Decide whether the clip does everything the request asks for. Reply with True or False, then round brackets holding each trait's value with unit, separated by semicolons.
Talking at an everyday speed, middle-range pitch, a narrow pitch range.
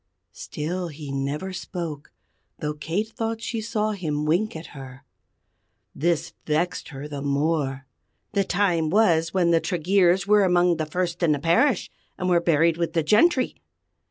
False (160 wpm; 170 Hz; 3.9 semitones)